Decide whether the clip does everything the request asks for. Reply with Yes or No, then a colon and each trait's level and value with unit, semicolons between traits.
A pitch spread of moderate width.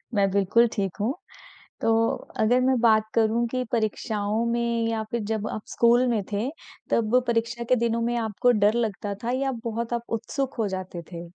No: narrow, 1.9 semitones